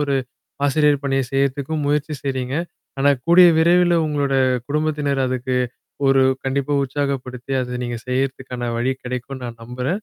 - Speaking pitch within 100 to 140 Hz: Yes, low, 135 Hz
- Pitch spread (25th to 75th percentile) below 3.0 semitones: Yes, narrow, 2.5 semitones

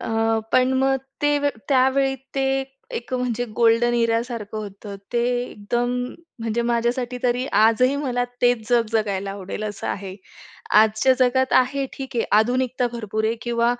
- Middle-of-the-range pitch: No, high, 240 Hz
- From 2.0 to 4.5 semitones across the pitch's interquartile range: Yes, narrow, 2.5 semitones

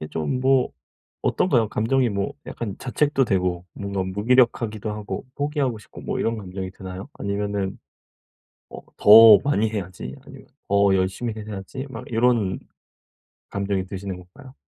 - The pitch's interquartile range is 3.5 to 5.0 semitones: Yes, average, 4.1 semitones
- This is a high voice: No, low, 105 Hz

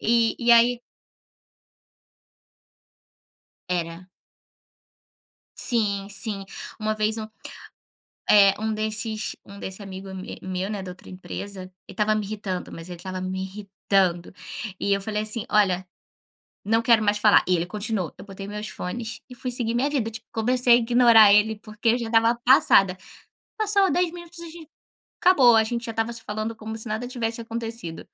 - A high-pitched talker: Yes, high, 215 Hz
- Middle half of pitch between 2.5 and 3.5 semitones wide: Yes, average, 3.0 semitones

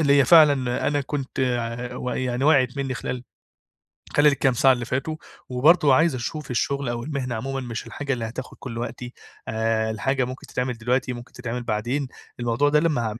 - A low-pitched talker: Yes, low, 130 Hz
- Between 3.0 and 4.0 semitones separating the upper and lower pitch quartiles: No, narrow, 2.6 semitones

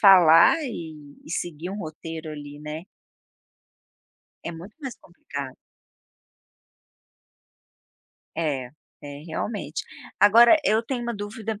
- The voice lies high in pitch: No, medium, 170 Hz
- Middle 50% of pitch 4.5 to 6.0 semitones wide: Yes, wide, 5.6 semitones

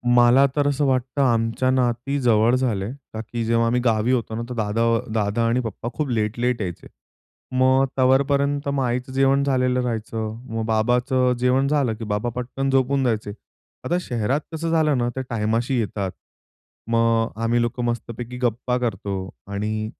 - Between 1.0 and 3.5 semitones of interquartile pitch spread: Yes, average, 2.7 semitones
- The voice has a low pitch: Yes, low, 120 Hz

